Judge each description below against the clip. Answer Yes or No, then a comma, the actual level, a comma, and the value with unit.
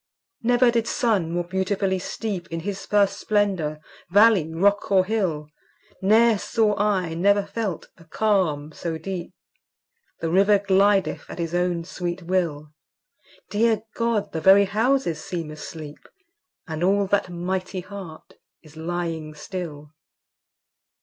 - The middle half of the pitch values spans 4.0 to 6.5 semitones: No, average, 3.6 semitones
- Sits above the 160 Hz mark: Yes, medium, 185 Hz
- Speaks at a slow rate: Yes, slow, 130 wpm